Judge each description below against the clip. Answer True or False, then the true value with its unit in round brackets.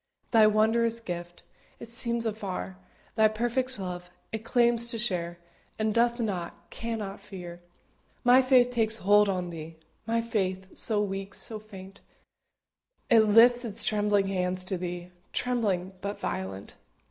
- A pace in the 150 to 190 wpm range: False (140 wpm)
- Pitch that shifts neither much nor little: True (3.9 semitones)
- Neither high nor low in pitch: False (210 Hz)